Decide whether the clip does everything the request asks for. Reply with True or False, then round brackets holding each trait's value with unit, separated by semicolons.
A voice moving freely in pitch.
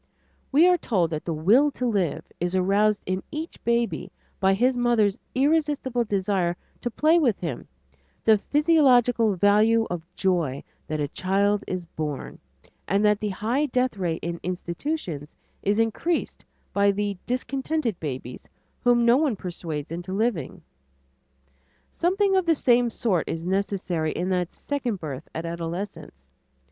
True (5.9 semitones)